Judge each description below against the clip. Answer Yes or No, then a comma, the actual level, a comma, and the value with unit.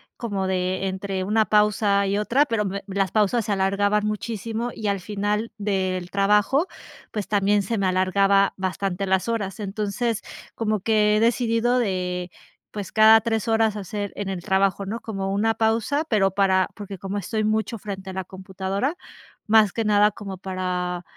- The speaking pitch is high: Yes, high, 205 Hz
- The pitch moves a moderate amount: No, narrow, 2.2 semitones